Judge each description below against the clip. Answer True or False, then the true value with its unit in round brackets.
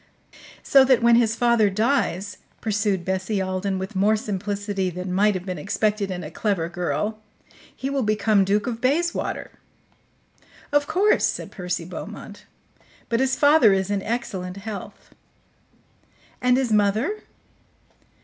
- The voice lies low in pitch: False (205 Hz)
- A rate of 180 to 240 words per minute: False (140 wpm)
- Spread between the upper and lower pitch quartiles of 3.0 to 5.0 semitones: True (3.8 semitones)